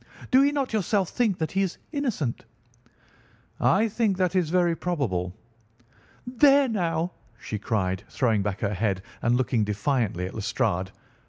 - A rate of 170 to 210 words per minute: No, average, 155 wpm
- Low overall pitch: No, medium, 160 Hz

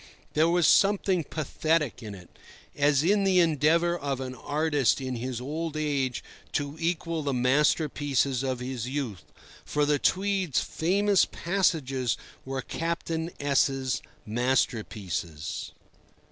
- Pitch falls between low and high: Yes, medium, 145 Hz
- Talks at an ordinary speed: No, slow, 120 wpm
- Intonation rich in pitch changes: No, average, 4.4 semitones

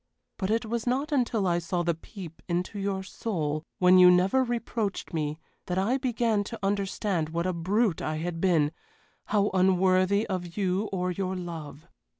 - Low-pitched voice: No, medium, 185 Hz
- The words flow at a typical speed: Yes, average, 170 wpm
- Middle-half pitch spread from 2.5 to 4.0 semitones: Yes, average, 3.4 semitones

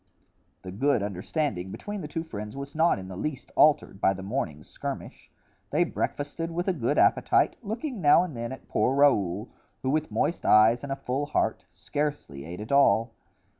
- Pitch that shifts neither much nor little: No, wide, 6.9 semitones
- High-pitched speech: No, low, 135 Hz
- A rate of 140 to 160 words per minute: No, average, 185 wpm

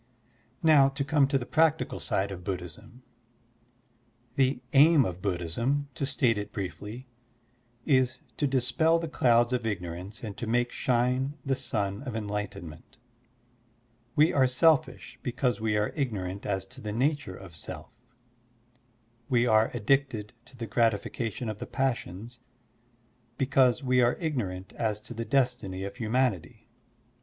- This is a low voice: Yes, low, 120 Hz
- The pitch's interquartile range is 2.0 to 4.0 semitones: No, average, 4.6 semitones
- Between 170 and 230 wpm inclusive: No, average, 140 wpm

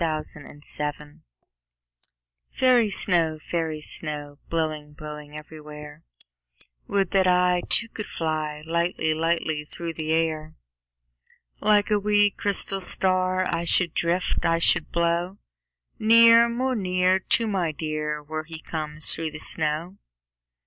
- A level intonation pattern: No, average, 3.3 semitones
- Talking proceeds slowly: Yes, slow, 125 wpm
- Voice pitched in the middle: Yes, medium, 165 Hz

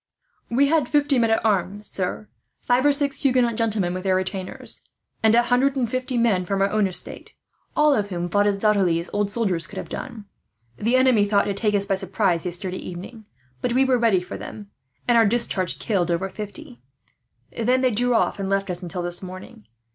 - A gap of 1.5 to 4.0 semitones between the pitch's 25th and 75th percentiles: No, average, 4.5 semitones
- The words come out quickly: Yes, fast, 210 wpm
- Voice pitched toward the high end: Yes, high, 210 Hz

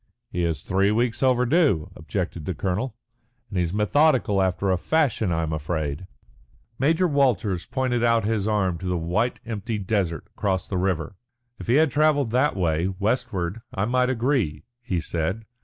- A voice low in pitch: Yes, low, 100 Hz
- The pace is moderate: Yes, average, 165 wpm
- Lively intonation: Yes, wide, 5.8 semitones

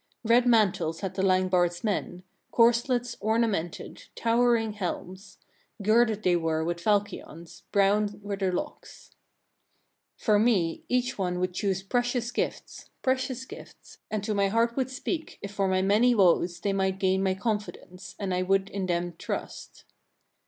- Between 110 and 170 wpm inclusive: Yes, average, 150 wpm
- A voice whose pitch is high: Yes, high, 200 Hz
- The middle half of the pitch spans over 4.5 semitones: No, average, 3.9 semitones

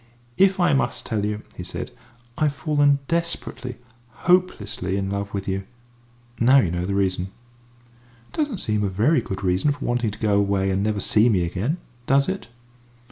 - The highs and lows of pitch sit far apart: Yes, wide, 6.8 semitones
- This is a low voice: Yes, low, 105 Hz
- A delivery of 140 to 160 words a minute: No, average, 180 wpm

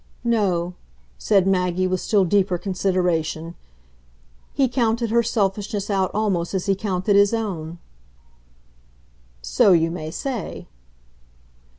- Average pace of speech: No, slow, 110 wpm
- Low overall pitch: No, high, 195 Hz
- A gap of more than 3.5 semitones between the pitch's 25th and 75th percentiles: No, average, 3.0 semitones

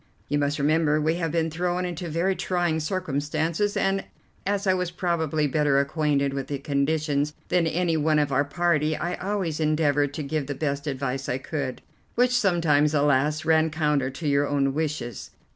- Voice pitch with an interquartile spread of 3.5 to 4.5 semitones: No, average, 3.0 semitones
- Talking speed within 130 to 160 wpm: No, average, 175 wpm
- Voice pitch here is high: No, medium, 155 Hz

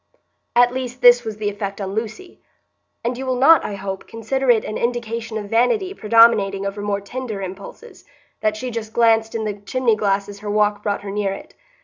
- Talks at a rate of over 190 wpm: Yes, fast, 205 wpm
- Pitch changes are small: No, average, 3.0 semitones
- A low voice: No, high, 220 Hz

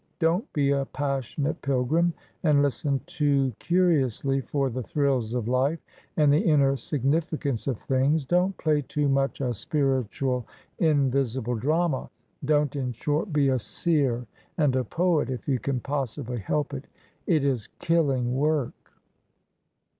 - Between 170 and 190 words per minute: No, average, 140 wpm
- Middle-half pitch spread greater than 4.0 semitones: No, average, 2.8 semitones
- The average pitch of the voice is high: No, medium, 140 Hz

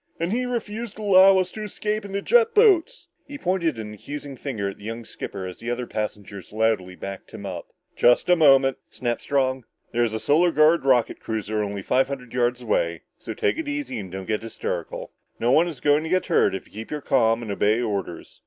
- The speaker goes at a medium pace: No, fast, 220 wpm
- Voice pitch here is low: Yes, low, 130 Hz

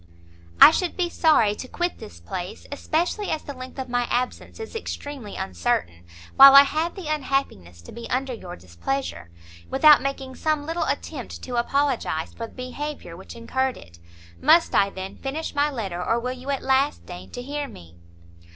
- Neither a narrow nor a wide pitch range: No, wide, 6.2 semitones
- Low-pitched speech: No, very high, 265 Hz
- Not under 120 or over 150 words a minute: No, average, 180 wpm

